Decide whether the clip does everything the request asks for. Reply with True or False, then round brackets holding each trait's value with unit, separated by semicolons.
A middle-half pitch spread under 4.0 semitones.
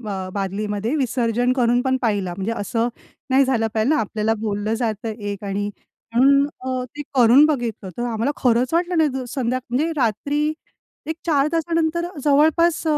False (4.8 semitones)